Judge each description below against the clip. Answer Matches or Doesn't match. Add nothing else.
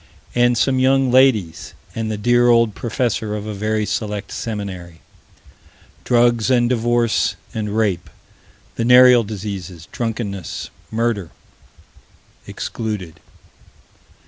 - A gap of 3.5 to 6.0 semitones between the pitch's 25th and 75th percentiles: Doesn't match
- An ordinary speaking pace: Doesn't match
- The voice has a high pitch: Doesn't match